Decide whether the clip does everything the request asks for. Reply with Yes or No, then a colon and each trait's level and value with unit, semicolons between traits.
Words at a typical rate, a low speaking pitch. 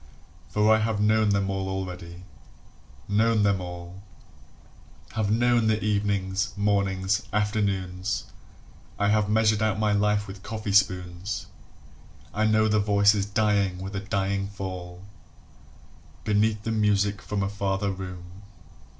No: slow, 130 wpm; low, 100 Hz